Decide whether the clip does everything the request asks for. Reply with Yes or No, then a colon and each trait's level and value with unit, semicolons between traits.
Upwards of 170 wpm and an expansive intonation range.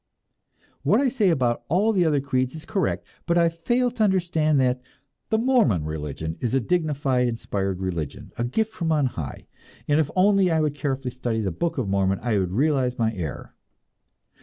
Yes: average, 190 wpm; wide, 7.4 semitones